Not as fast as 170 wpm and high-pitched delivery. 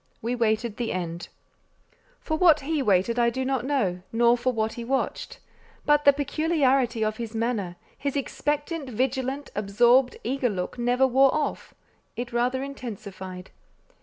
Yes: average, 150 wpm; high, 245 Hz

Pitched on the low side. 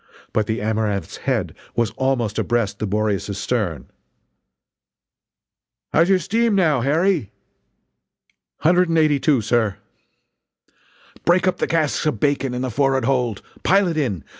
Yes: low, 130 Hz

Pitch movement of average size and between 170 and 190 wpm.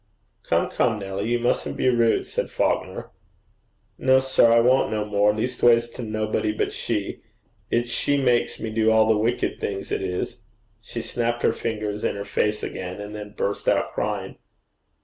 No: narrow, 2.3 semitones; average, 175 wpm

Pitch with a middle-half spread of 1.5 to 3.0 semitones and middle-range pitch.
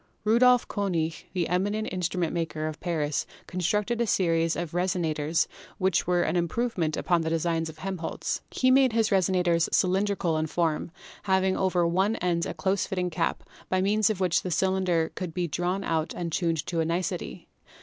Yes: narrow, 2.5 semitones; medium, 180 Hz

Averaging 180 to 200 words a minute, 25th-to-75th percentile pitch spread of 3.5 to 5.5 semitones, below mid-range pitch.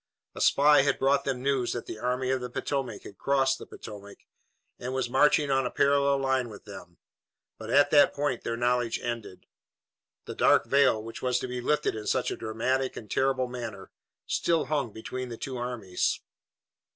No: average, 190 wpm; average, 2.7 semitones; low, 125 Hz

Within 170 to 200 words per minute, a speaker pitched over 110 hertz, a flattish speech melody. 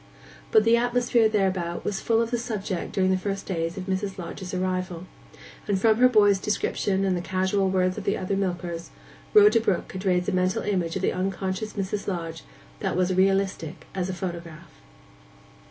Yes: average, 185 wpm; high, 190 Hz; narrow, 2.0 semitones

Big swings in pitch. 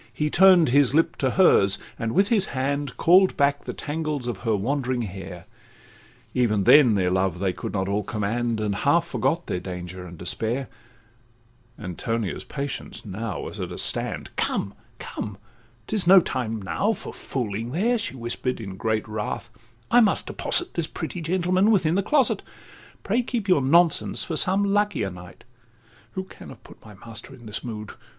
Yes: wide, 8.3 semitones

